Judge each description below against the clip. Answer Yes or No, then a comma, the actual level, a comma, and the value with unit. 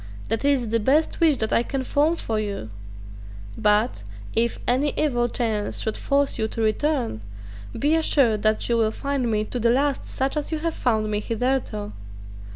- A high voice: Yes, high, 240 Hz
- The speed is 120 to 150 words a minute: No, average, 180 wpm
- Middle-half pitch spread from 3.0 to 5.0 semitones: Yes, average, 4.6 semitones